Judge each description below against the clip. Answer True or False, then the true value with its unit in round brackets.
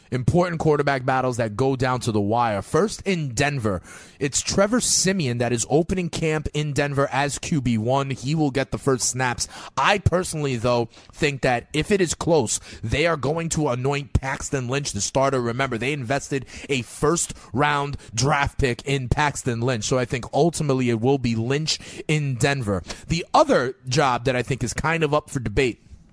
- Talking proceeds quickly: False (185 wpm)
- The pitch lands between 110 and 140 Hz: True (135 Hz)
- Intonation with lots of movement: False (3.6 semitones)